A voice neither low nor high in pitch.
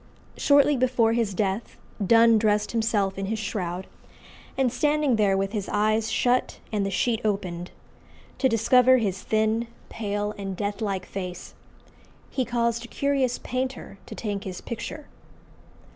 No: high, 220 Hz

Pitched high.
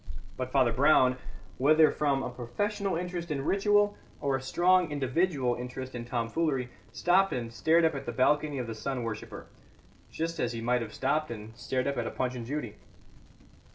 No: low, 135 Hz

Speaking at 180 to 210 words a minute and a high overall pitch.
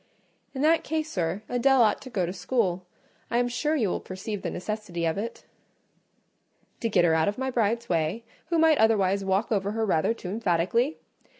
Yes: average, 195 wpm; high, 215 Hz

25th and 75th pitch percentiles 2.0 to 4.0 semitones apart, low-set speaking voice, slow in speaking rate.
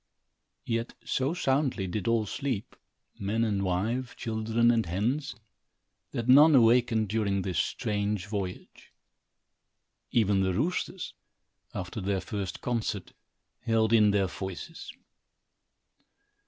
Yes: average, 3.4 semitones; low, 110 Hz; slow, 110 wpm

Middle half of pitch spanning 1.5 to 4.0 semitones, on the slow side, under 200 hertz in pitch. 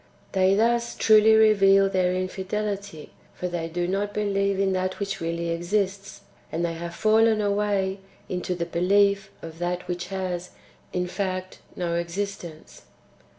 No: narrow, 2.4 semitones; average, 145 wpm; high, 190 Hz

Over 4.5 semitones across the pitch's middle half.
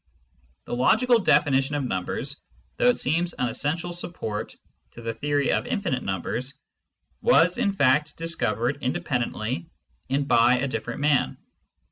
Yes: average, 5.2 semitones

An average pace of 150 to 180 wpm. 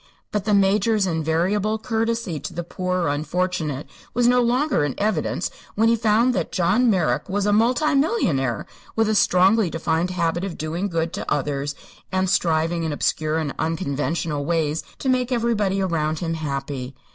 Yes: average, 170 wpm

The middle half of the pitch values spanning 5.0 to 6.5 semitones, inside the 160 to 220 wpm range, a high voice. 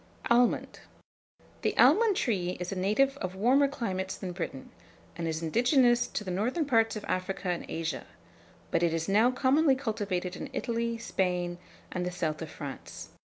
Yes: wide, 5.5 semitones; average, 165 wpm; high, 195 Hz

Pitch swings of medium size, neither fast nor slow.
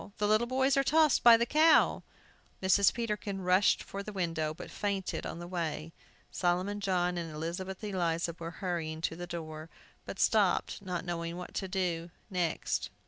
Yes: average, 3.4 semitones; average, 170 wpm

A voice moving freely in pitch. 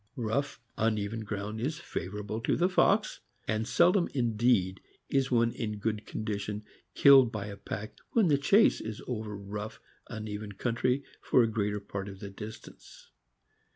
No: average, 3.2 semitones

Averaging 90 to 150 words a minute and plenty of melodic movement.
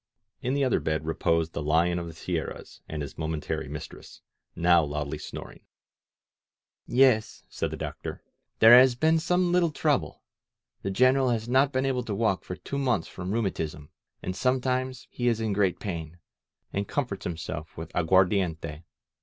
No: average, 165 wpm; wide, 7.7 semitones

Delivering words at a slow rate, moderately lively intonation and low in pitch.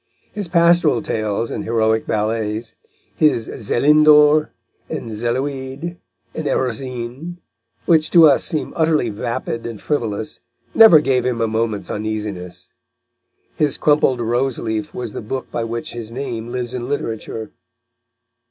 Yes: slow, 130 wpm; average, 4.9 semitones; low, 120 Hz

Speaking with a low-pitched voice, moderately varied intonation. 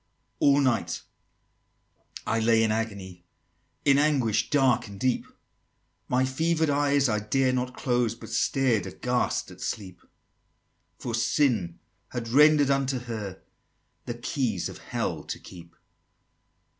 Yes: low, 125 Hz; average, 3.9 semitones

